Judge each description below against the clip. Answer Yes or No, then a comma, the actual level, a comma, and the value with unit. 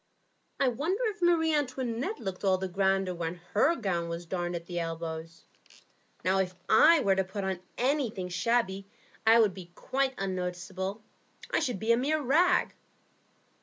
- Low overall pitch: No, high, 195 Hz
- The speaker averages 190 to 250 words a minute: No, average, 165 wpm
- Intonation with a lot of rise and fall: Yes, wide, 6.3 semitones